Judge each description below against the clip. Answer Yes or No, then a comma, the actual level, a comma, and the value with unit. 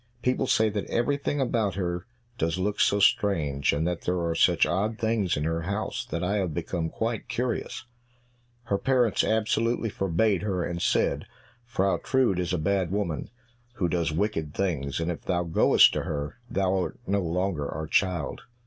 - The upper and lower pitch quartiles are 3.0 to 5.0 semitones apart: Yes, average, 4.3 semitones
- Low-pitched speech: Yes, very low, 95 Hz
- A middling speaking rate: Yes, average, 175 wpm